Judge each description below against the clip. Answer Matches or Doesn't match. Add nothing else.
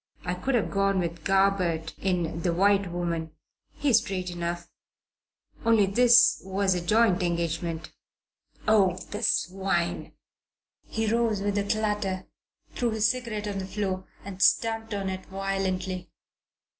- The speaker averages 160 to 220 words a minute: Doesn't match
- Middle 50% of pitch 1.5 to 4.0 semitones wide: Matches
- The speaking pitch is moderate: Doesn't match